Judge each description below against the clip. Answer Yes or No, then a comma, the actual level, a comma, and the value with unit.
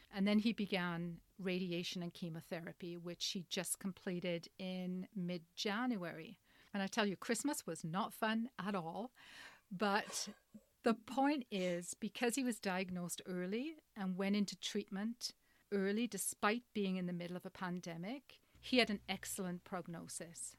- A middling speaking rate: Yes, average, 150 wpm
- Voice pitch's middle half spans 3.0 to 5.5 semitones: Yes, average, 3.4 semitones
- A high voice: Yes, high, 195 Hz